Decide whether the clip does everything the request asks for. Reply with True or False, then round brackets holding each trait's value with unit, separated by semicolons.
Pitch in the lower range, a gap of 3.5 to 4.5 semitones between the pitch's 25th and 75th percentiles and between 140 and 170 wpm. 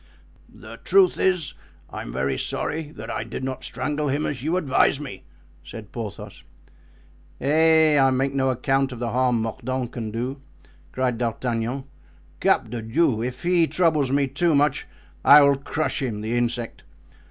True (130 Hz; 3.8 semitones; 160 wpm)